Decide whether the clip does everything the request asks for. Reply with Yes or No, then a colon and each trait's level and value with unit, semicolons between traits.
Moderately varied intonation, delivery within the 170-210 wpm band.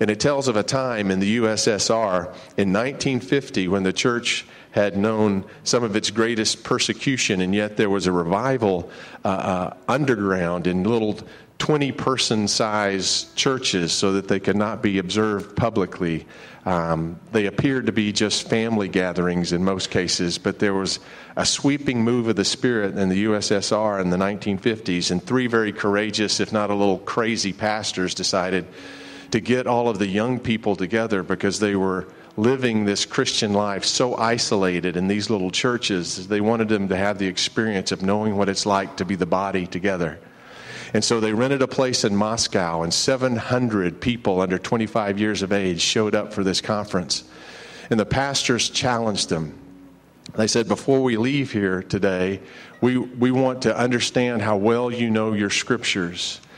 Yes: average, 3.7 semitones; average, 175 wpm